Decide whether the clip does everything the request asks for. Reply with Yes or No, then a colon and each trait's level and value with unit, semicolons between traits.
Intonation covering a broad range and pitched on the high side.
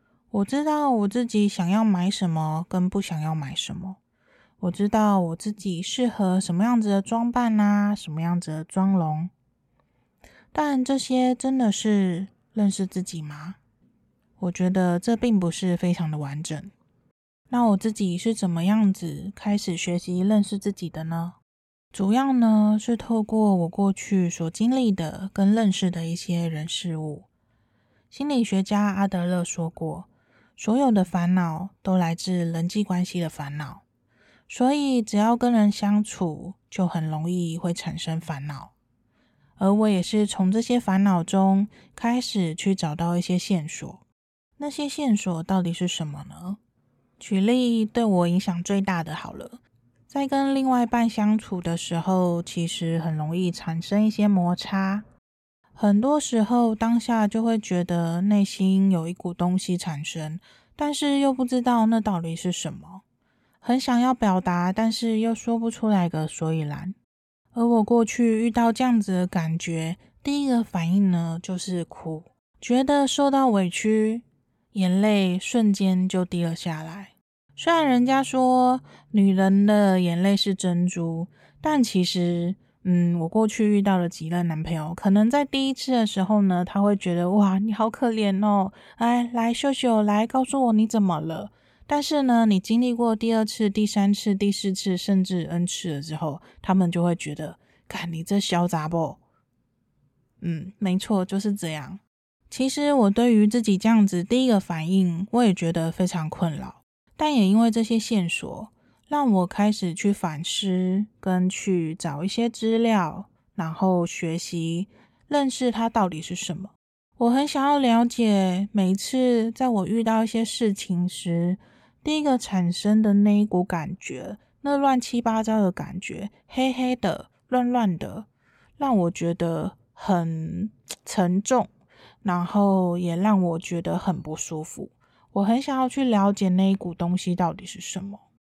No: average, 4.4 semitones; high, 195 Hz